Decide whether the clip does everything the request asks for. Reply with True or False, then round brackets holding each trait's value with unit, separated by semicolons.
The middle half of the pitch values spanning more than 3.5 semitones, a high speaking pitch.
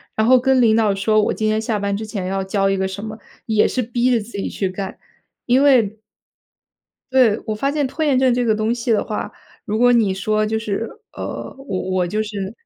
False (3.2 semitones; 220 Hz)